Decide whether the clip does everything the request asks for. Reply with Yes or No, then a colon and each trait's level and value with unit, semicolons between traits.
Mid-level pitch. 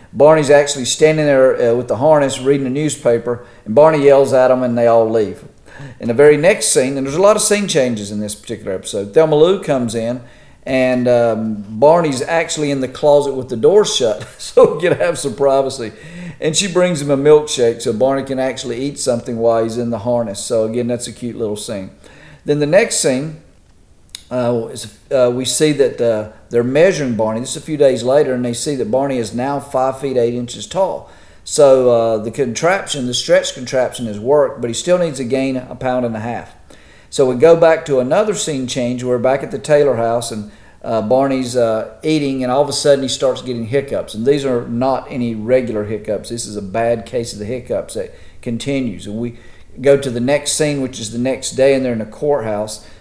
No: low, 125 Hz